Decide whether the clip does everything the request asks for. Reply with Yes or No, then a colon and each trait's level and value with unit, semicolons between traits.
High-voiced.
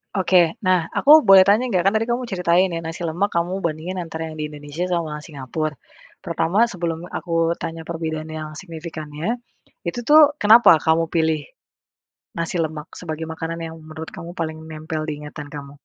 No: medium, 165 Hz